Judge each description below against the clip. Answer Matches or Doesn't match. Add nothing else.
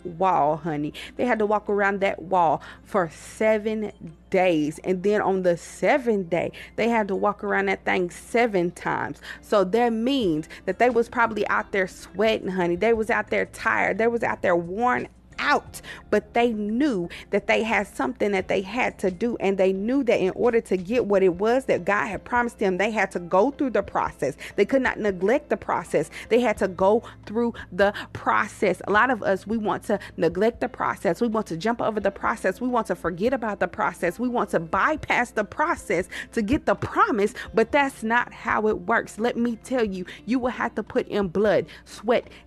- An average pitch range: Matches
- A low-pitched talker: Doesn't match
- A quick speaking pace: Matches